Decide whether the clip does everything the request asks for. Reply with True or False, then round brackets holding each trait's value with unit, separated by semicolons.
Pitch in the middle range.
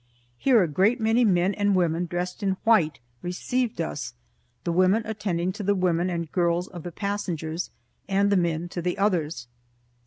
True (180 Hz)